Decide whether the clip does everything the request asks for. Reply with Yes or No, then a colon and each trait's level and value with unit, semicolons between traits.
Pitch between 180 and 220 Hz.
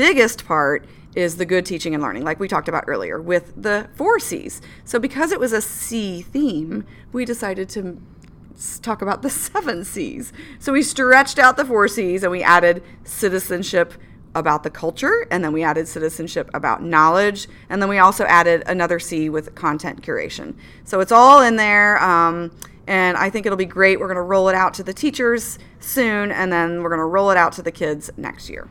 Yes: high, 190 Hz